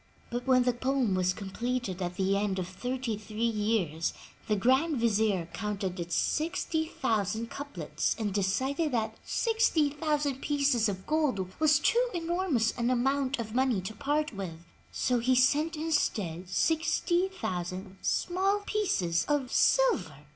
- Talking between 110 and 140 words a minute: Yes, slow, 135 wpm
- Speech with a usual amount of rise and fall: No, wide, 7.2 semitones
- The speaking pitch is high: Yes, high, 240 Hz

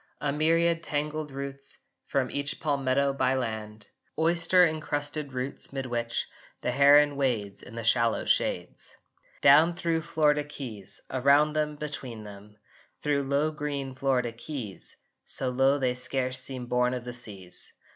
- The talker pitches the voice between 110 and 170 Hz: Yes, medium, 140 Hz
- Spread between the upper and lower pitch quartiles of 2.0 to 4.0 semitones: Yes, average, 3.2 semitones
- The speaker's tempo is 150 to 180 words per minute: No, average, 140 wpm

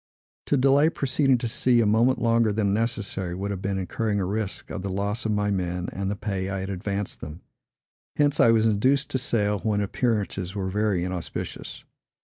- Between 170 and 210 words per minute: Yes, average, 200 wpm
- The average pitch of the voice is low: Yes, low, 105 Hz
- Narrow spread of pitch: No, average, 3.1 semitones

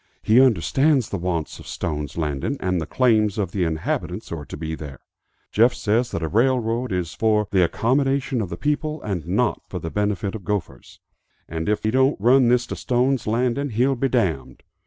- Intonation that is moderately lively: No, wide, 6.8 semitones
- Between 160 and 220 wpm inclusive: Yes, average, 200 wpm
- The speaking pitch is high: No, low, 105 Hz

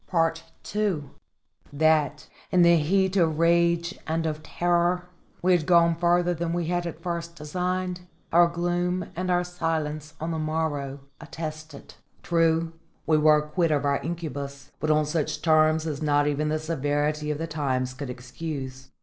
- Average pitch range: No, narrow, 2.3 semitones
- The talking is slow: No, average, 160 wpm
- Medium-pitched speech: Yes, medium, 160 Hz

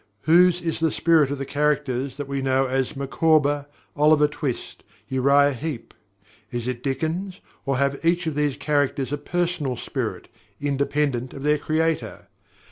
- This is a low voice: No, medium, 145 Hz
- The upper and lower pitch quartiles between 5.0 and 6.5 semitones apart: No, average, 2.7 semitones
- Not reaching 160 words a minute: Yes, average, 150 wpm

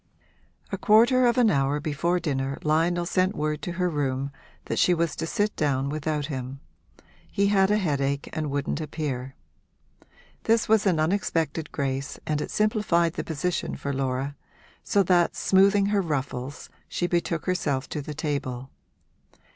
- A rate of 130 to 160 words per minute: Yes, average, 155 wpm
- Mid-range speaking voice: Yes, medium, 155 Hz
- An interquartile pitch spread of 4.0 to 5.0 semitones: Yes, average, 4.6 semitones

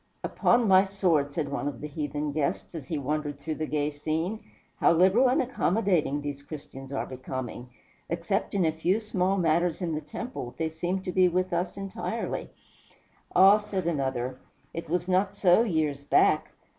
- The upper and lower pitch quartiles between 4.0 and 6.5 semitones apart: Yes, average, 4.5 semitones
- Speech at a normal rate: Yes, average, 175 wpm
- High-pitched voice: No, medium, 165 Hz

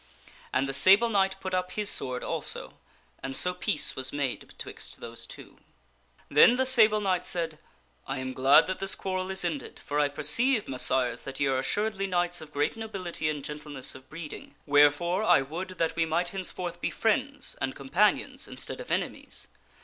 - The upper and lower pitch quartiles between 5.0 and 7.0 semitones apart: Yes, wide, 5.5 semitones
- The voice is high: No, medium, 170 Hz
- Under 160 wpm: No, average, 185 wpm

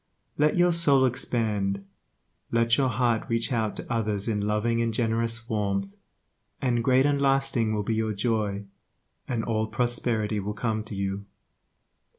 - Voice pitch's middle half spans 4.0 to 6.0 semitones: No, narrow, 2.6 semitones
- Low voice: Yes, low, 115 Hz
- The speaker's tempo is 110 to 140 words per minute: No, average, 155 wpm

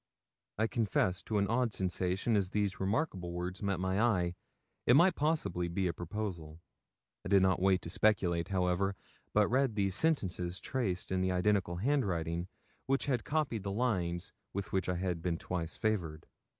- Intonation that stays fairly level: No, average, 3.5 semitones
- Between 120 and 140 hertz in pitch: No, very low, 95 Hz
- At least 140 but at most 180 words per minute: Yes, average, 170 wpm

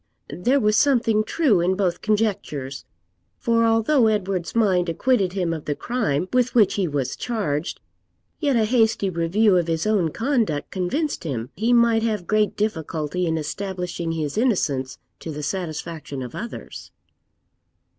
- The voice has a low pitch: No, high, 195 Hz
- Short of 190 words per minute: Yes, average, 150 wpm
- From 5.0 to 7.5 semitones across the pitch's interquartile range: Yes, wide, 5.6 semitones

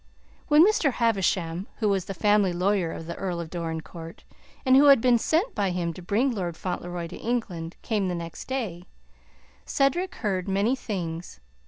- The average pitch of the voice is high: Yes, high, 195 Hz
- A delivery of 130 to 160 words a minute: No, average, 175 wpm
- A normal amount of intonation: No, wide, 5.7 semitones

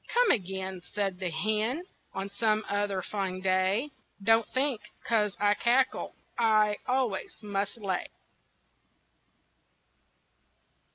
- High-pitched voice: Yes, high, 205 Hz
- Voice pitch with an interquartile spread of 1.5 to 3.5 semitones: Yes, average, 2.9 semitones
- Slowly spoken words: Yes, slow, 105 wpm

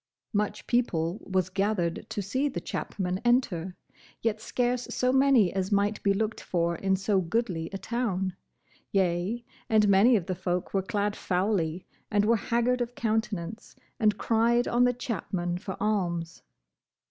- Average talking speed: Yes, average, 155 wpm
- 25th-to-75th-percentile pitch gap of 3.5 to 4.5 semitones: Yes, average, 4.1 semitones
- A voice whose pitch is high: Yes, high, 205 Hz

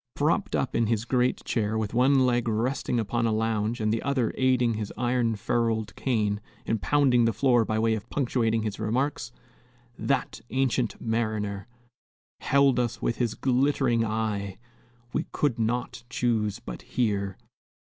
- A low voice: Yes, low, 115 Hz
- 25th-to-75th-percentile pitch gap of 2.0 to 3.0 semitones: Yes, narrow, 2.4 semitones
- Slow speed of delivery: No, average, 155 wpm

